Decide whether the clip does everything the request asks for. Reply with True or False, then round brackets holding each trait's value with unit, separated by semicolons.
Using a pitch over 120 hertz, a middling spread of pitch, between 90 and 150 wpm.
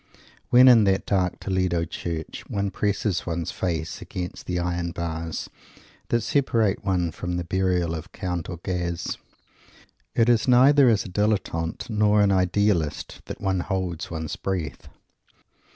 False (90 Hz; 3.3 semitones; 140 wpm)